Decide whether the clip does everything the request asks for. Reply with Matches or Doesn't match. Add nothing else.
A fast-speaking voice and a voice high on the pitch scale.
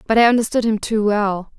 Matches